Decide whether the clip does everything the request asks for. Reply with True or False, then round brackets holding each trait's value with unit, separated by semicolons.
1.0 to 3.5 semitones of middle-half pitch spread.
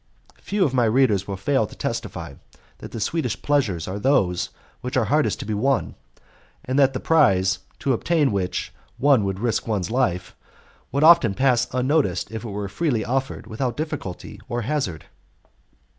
False (5.5 semitones)